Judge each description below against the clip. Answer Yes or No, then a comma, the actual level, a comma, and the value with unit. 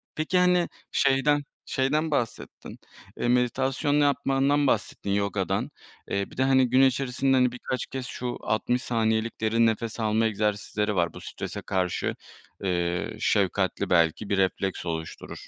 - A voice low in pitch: Yes, low, 120 Hz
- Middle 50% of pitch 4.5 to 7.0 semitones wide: Yes, average, 4.8 semitones